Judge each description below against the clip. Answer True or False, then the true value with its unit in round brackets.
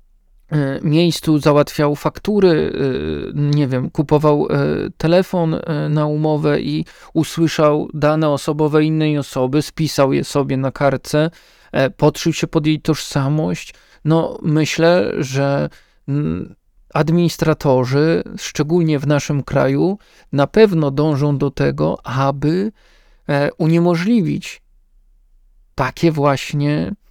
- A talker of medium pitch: True (150 Hz)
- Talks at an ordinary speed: False (95 wpm)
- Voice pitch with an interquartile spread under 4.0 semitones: True (2.4 semitones)